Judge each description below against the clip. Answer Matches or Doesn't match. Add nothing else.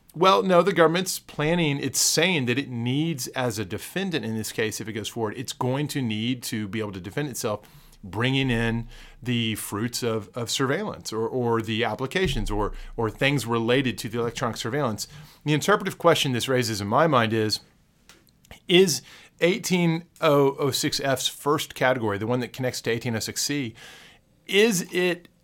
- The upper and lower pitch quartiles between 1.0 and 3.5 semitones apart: Doesn't match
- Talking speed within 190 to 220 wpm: Doesn't match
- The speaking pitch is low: Matches